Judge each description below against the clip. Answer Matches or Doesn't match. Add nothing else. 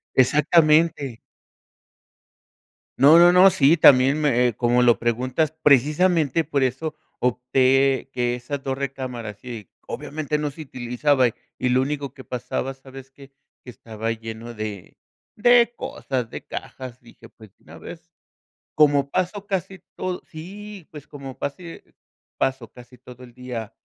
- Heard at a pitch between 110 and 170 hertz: Matches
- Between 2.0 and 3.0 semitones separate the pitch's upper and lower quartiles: Doesn't match